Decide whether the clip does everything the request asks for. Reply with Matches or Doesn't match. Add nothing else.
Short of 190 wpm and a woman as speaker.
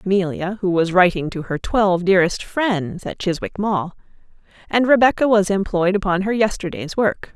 Matches